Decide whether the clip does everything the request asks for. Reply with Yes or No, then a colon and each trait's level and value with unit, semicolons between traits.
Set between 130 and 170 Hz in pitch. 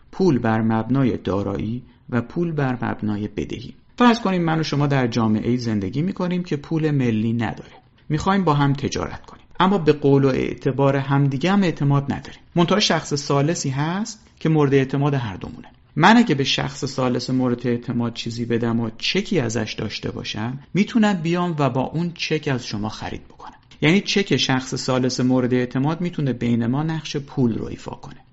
Yes: medium, 140 Hz